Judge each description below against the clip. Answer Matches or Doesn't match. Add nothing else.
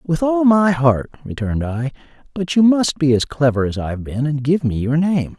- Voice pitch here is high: Doesn't match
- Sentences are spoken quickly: Matches